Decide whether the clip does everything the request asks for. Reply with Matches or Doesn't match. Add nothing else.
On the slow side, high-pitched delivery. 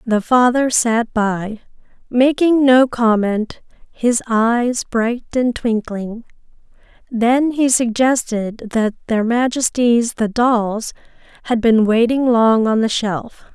Matches